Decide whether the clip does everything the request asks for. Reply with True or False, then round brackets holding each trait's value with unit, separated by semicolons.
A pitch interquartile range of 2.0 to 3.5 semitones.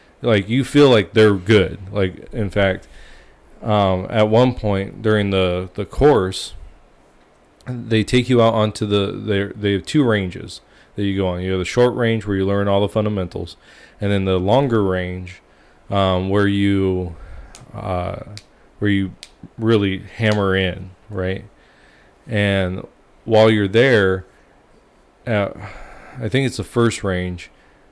True (2.6 semitones)